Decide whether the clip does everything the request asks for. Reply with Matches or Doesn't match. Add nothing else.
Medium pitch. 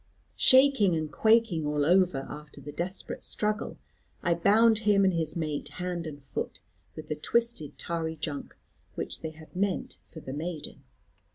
Matches